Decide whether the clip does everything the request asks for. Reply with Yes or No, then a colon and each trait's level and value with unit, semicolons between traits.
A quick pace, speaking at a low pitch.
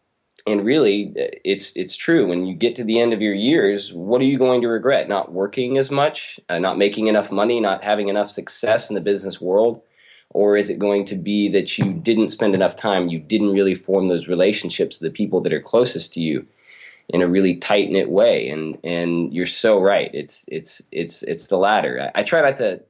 Yes: fast, 225 wpm; low, 100 Hz